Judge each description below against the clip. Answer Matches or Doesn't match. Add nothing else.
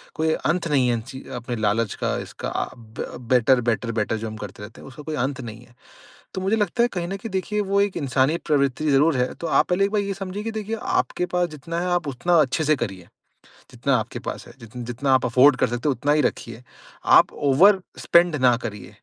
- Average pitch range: Doesn't match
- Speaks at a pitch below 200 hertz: Matches